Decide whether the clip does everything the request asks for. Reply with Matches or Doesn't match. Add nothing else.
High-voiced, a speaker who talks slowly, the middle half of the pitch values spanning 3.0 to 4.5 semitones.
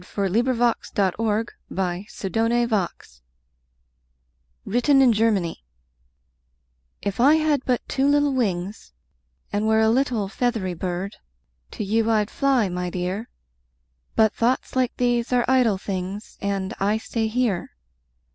Matches